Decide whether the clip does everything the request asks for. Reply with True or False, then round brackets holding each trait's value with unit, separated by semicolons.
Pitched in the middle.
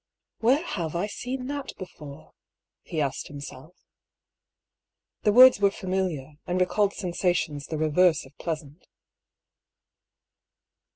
True (180 Hz)